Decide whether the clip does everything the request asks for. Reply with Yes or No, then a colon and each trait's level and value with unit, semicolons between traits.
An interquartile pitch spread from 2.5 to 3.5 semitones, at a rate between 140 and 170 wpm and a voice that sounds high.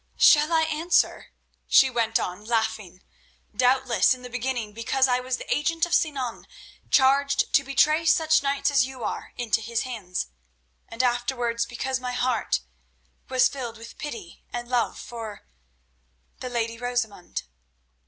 Yes: average, 2.9 semitones; average, 145 wpm; high, 245 Hz